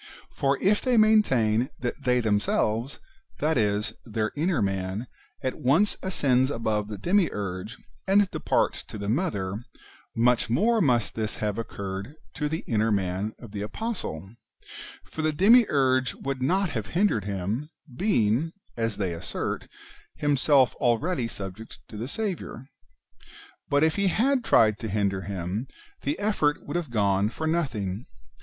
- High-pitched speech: No, low, 120 Hz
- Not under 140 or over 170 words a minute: Yes, average, 145 wpm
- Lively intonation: Yes, wide, 7.3 semitones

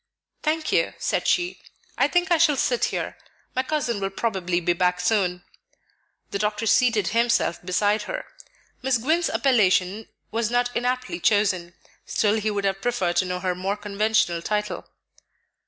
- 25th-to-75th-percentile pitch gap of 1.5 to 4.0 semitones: No, average, 4.8 semitones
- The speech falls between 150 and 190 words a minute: Yes, average, 155 wpm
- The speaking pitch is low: No, high, 210 Hz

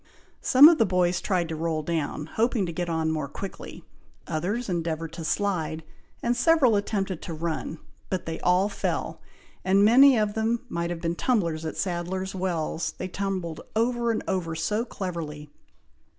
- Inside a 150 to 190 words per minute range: Yes, average, 165 wpm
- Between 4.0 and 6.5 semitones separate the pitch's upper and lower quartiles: Yes, average, 4.3 semitones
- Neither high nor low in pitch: Yes, medium, 180 Hz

